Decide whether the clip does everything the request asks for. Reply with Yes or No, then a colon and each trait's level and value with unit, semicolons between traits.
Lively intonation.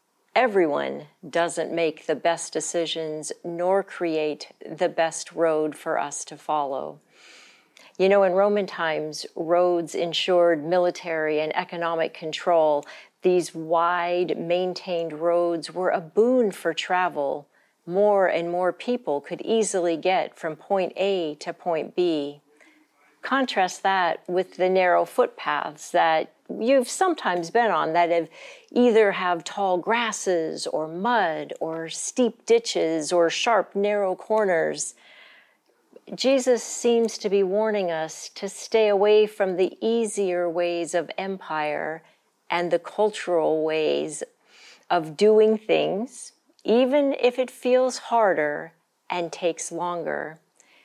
No: average, 4.0 semitones